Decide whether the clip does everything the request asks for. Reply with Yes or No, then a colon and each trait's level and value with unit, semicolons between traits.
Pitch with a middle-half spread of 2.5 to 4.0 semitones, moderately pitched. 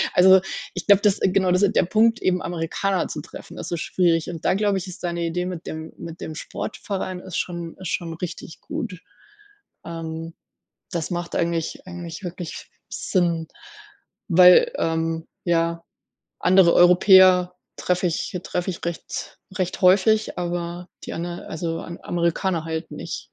No: narrow, 1.9 semitones; medium, 175 Hz